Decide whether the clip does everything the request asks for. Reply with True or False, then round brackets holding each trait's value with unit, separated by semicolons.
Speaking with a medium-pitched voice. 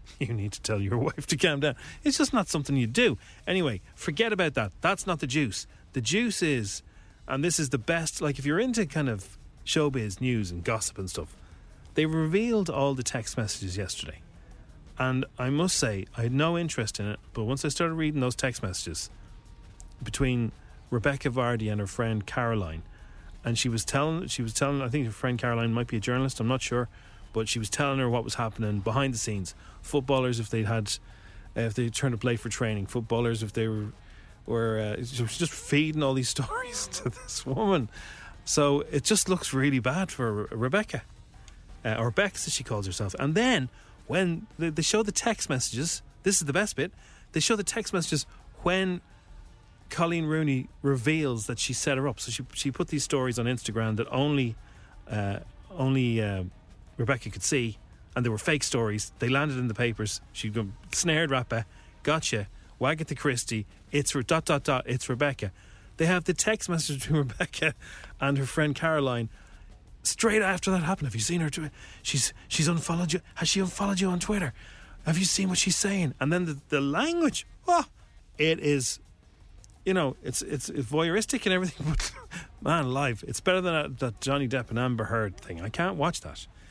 False (130 Hz)